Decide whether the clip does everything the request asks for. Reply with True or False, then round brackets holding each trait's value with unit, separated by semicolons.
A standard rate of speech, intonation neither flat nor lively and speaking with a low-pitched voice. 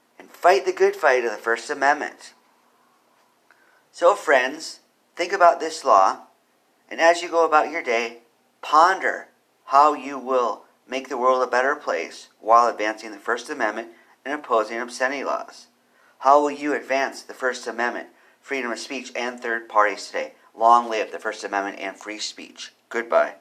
True (160 wpm; 4.2 semitones; 130 Hz)